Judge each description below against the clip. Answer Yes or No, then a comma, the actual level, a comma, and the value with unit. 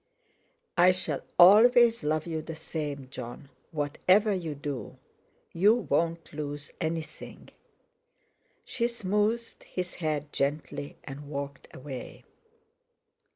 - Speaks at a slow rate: Yes, slow, 105 wpm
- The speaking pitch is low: No, medium, 160 Hz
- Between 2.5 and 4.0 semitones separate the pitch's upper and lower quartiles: No, average, 4.6 semitones